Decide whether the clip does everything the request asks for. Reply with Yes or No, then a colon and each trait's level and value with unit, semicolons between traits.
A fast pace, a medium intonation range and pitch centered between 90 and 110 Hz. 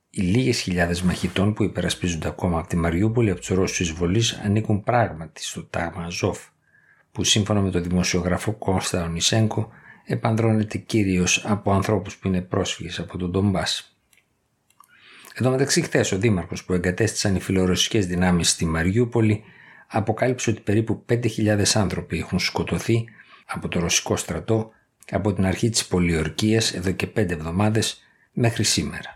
No: average, 145 wpm; average, 3.6 semitones; low, 100 Hz